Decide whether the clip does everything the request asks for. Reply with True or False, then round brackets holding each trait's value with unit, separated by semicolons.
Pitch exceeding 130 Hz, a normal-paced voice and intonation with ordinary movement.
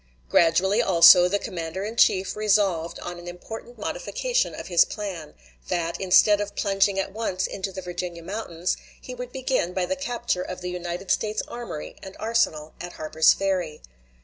True (190 Hz; 170 wpm; 3.4 semitones)